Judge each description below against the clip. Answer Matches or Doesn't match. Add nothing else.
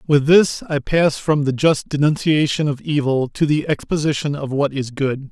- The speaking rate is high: Doesn't match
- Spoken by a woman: Doesn't match